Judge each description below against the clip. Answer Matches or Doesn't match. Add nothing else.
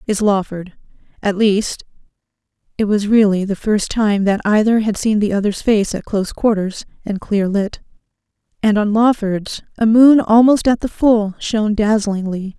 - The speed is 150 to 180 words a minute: Matches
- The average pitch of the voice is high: Matches